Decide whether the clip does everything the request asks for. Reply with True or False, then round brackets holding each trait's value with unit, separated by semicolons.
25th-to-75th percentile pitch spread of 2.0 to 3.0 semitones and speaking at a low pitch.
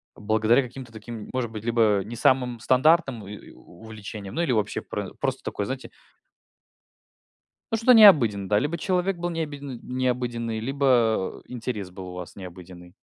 False (4.3 semitones; 120 Hz)